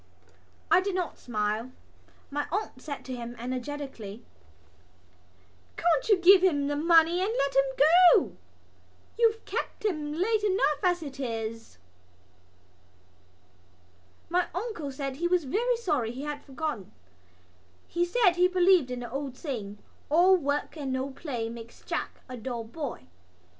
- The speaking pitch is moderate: No, very high, 290 Hz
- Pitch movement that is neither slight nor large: No, wide, 5.9 semitones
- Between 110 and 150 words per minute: Yes, average, 140 wpm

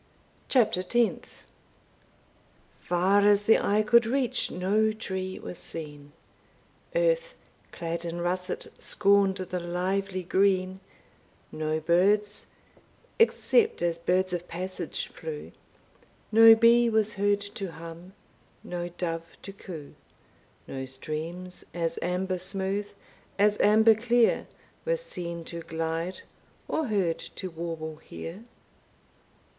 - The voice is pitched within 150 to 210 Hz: Yes, medium, 185 Hz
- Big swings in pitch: No, average, 3.6 semitones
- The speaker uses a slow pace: Yes, slow, 110 wpm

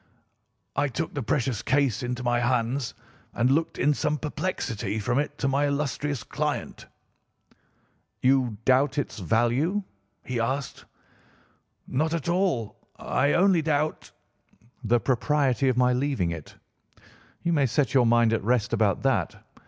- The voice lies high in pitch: No, low, 130 Hz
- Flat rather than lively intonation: No, average, 3.5 semitones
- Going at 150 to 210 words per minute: No, average, 140 wpm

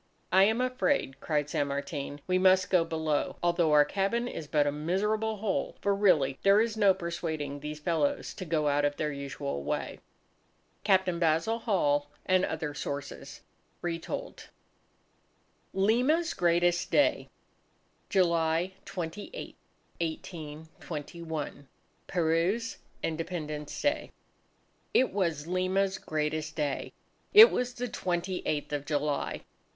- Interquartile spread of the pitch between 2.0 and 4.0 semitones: No, average, 4.4 semitones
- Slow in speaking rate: Yes, slow, 120 wpm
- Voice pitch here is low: No, medium, 170 Hz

